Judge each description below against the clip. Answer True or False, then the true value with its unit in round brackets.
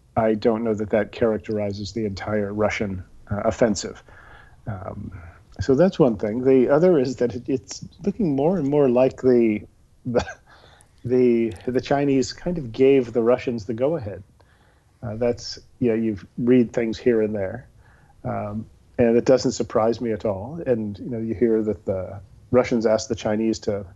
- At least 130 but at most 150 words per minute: False (170 wpm)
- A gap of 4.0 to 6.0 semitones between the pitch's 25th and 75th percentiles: False (2.9 semitones)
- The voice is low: True (115 Hz)